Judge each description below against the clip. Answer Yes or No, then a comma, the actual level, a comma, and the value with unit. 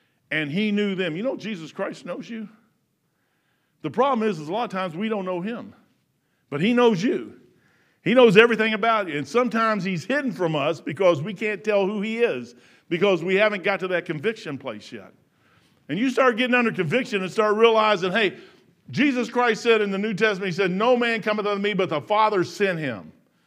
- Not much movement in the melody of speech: No, average, 3.7 semitones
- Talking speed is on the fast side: Yes, fast, 210 wpm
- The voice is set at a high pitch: Yes, high, 210 Hz